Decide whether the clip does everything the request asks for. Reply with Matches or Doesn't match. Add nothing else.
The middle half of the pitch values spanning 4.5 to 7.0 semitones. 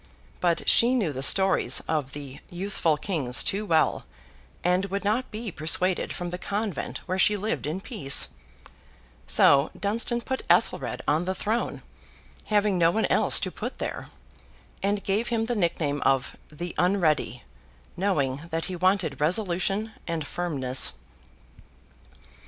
Matches